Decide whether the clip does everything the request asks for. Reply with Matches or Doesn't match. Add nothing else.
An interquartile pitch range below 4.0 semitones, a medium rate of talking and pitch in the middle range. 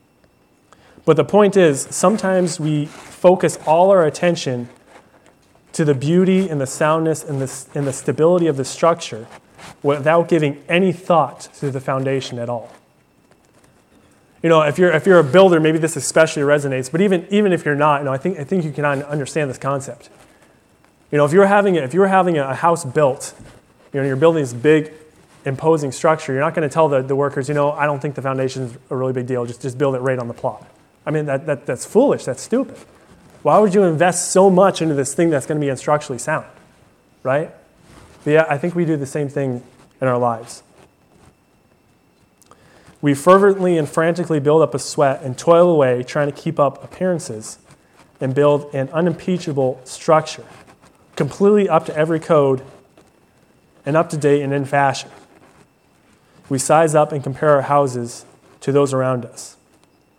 Matches